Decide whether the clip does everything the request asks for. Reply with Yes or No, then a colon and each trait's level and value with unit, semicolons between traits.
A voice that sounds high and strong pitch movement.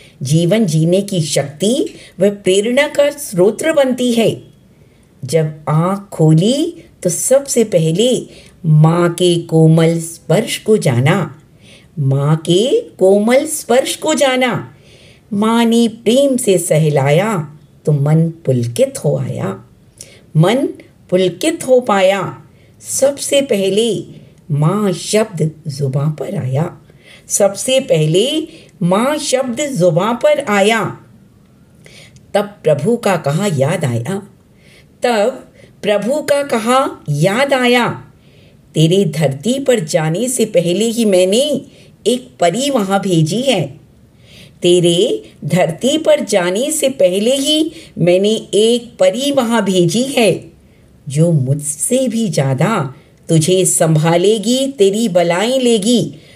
Yes: high, 195 Hz; wide, 7.3 semitones